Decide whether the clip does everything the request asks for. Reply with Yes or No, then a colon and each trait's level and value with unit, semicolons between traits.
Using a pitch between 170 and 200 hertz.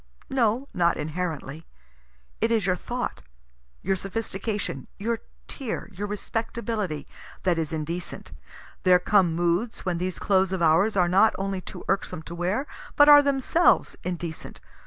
Yes: high, 190 Hz